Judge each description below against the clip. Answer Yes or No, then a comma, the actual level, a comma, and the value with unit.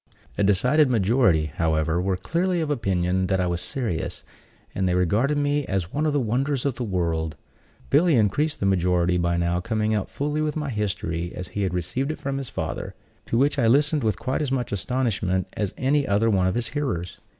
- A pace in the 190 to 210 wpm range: Yes, fast, 205 wpm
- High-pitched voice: No, low, 105 Hz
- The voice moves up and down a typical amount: No, wide, 7.3 semitones